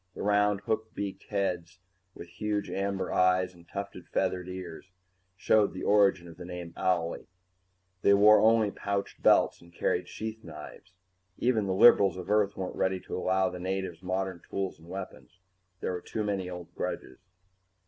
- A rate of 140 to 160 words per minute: No, average, 170 wpm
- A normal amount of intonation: No, narrow, 2.0 semitones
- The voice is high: No, very low, 95 Hz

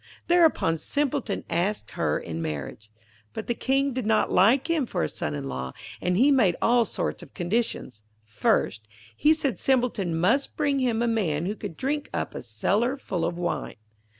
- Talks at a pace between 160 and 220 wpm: Yes, average, 180 wpm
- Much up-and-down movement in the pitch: Yes, wide, 8.7 semitones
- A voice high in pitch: Yes, high, 215 Hz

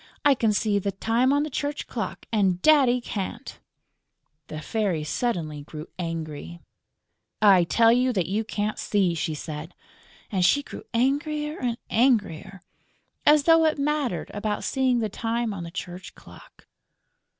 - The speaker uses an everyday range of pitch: No, wide, 6.6 semitones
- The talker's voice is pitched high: Yes, high, 215 Hz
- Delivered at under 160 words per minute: Yes, average, 150 wpm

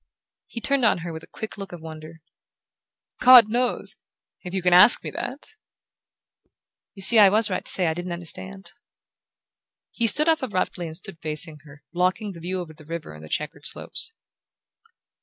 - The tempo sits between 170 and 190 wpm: Yes, average, 180 wpm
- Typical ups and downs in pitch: Yes, average, 4.9 semitones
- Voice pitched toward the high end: No, medium, 180 Hz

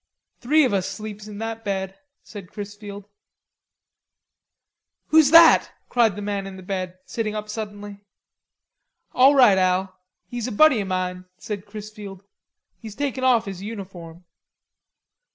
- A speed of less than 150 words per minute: Yes, slow, 135 wpm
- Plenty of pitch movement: No, average, 2.8 semitones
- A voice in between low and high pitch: No, high, 205 Hz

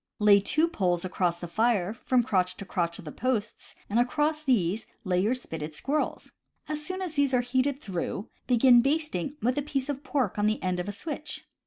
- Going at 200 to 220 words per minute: Yes, fast, 205 wpm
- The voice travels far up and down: Yes, wide, 6.9 semitones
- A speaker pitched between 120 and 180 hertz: No, high, 240 Hz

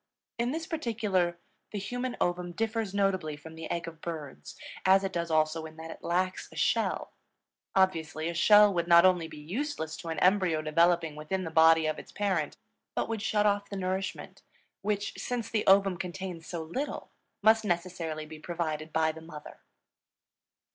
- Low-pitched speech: No, medium, 175 Hz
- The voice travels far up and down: No, average, 3.8 semitones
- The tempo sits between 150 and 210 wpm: Yes, average, 175 wpm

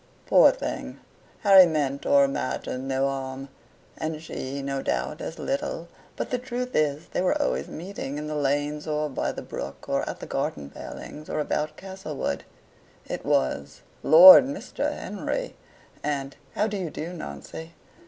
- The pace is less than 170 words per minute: Yes, average, 160 wpm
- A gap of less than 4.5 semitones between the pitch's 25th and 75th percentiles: No, average, 4.9 semitones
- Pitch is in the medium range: Yes, medium, 150 Hz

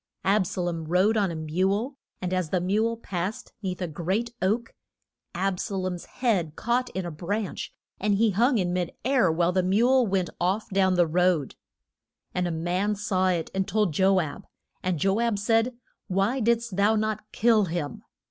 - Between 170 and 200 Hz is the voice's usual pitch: Yes, high, 190 Hz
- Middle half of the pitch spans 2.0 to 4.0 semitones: Yes, average, 3.4 semitones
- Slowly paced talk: No, average, 185 wpm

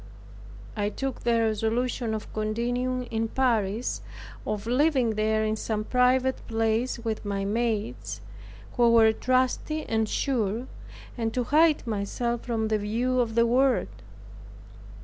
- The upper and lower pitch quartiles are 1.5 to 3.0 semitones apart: Yes, narrow, 2.5 semitones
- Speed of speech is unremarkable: No, slow, 130 wpm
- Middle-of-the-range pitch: No, high, 230 Hz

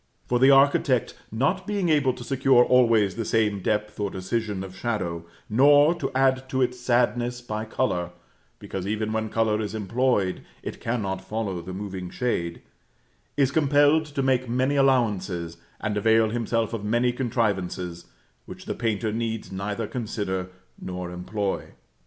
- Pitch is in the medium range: No, low, 115 Hz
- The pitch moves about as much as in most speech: Yes, average, 4.2 semitones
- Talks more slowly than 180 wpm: Yes, average, 150 wpm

